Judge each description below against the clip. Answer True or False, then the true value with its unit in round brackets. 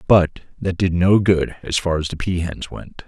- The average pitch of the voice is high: False (90 Hz)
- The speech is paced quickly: True (235 wpm)